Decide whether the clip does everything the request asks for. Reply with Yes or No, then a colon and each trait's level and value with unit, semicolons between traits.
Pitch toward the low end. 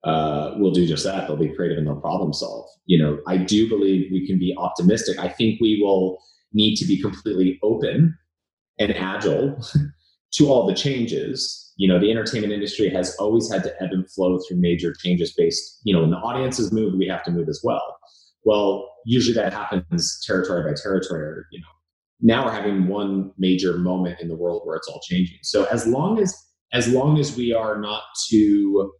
Yes: very low, 95 Hz